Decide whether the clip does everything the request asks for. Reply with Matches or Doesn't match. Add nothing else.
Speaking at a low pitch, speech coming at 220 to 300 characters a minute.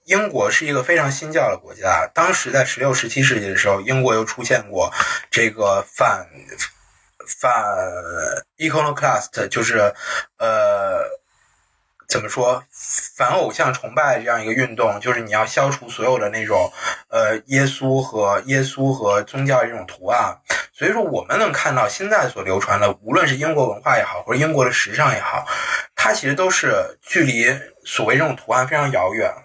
Matches